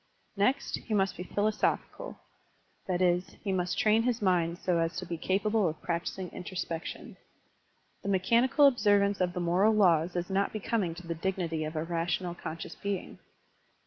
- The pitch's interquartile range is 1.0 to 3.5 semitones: Yes, average, 3.0 semitones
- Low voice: No, medium, 185 Hz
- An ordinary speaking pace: Yes, average, 170 wpm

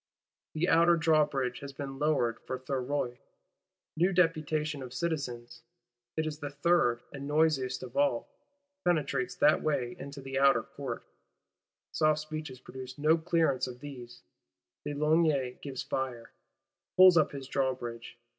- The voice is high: No, medium, 140 Hz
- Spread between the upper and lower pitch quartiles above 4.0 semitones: No, average, 3.3 semitones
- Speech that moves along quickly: No, slow, 135 wpm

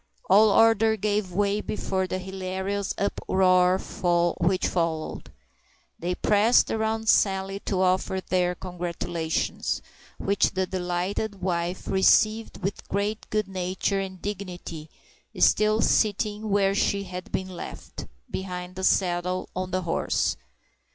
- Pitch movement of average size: No, narrow, 2.0 semitones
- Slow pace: Yes, slow, 115 wpm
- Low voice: No, high, 190 Hz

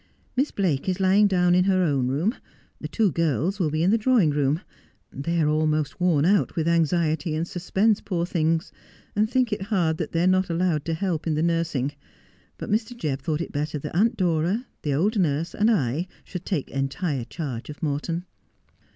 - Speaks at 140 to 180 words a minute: No, fast, 205 wpm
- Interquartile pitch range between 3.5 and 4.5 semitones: Yes, average, 3.8 semitones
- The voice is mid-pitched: Yes, medium, 170 Hz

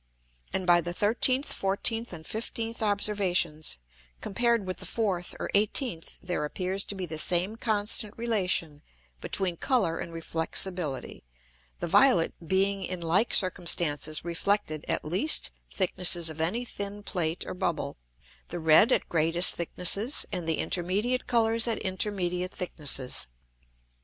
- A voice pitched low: No, medium, 185 Hz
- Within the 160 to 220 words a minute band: No, slow, 135 wpm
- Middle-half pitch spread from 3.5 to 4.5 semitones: Yes, average, 3.9 semitones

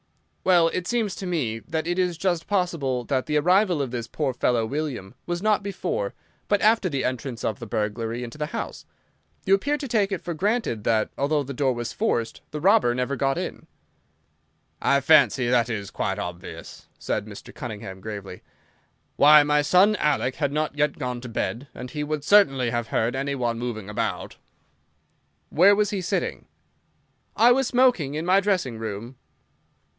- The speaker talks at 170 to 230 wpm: Yes, average, 180 wpm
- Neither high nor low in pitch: Yes, medium, 145 Hz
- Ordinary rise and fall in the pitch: No, wide, 7.4 semitones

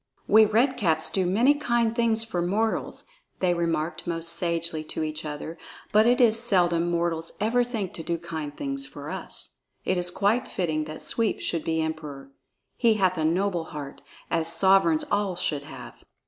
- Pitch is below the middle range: No, medium, 175 Hz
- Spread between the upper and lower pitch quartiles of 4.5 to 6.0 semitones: Yes, average, 5.1 semitones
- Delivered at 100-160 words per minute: No, average, 175 wpm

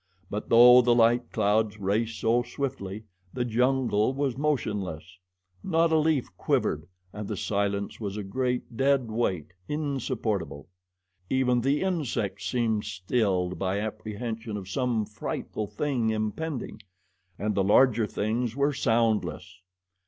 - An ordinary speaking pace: No, slow, 130 wpm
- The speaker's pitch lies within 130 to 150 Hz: No, low, 115 Hz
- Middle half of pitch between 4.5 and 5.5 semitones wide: No, average, 3.7 semitones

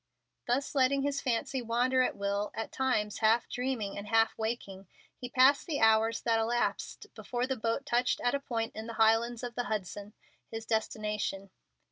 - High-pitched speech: Yes, high, 230 Hz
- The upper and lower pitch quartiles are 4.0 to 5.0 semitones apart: No, narrow, 2.4 semitones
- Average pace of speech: Yes, average, 175 wpm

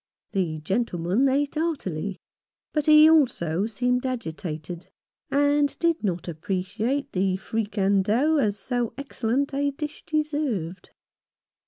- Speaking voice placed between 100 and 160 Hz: No, high, 230 Hz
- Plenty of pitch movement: Yes, wide, 7.2 semitones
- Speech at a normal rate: No, slow, 110 wpm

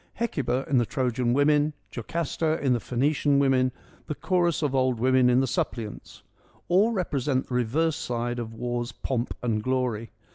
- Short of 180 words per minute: Yes, average, 160 wpm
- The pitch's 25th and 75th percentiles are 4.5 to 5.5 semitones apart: No, average, 3.4 semitones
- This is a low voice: Yes, low, 130 Hz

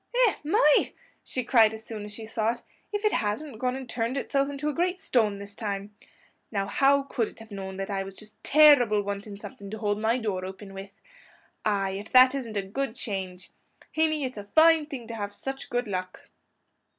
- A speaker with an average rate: No, fast, 210 wpm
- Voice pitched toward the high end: Yes, high, 220 Hz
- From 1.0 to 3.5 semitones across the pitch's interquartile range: No, average, 5.1 semitones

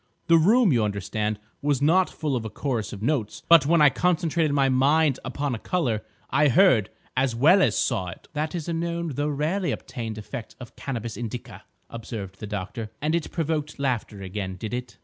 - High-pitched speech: No, low, 135 Hz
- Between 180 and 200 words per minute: Yes, average, 195 wpm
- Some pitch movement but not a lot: No, wide, 6.3 semitones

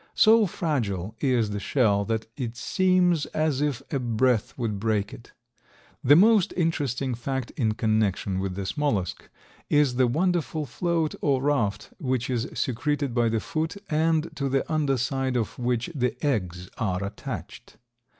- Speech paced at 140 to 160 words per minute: Yes, average, 155 wpm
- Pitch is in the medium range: No, low, 130 Hz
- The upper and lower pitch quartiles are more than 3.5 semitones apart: Yes, average, 5.3 semitones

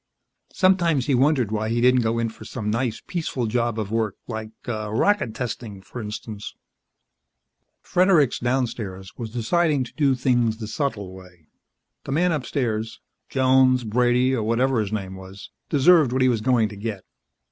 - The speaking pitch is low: Yes, low, 120 Hz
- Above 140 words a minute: Yes, average, 160 wpm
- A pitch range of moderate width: Yes, average, 3.4 semitones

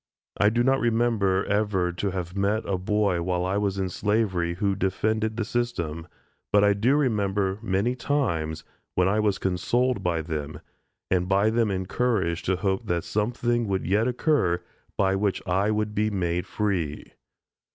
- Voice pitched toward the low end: Yes, low, 100 Hz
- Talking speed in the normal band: Yes, average, 170 wpm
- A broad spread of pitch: No, average, 3.2 semitones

